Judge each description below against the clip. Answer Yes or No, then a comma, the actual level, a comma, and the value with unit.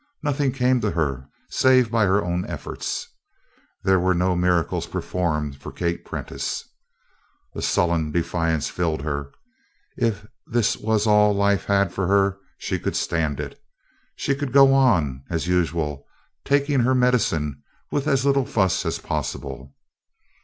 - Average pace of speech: Yes, average, 145 wpm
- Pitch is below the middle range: Yes, very low, 95 Hz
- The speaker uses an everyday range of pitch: No, wide, 7.1 semitones